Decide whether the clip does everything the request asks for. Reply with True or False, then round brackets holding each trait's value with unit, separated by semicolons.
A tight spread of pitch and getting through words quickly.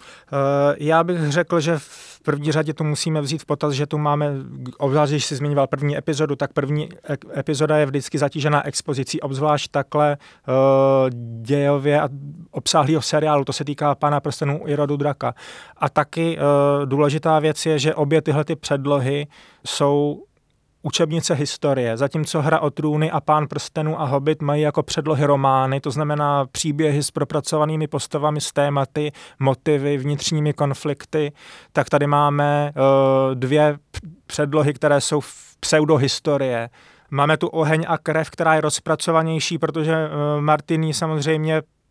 False (1.5 semitones; 150 wpm)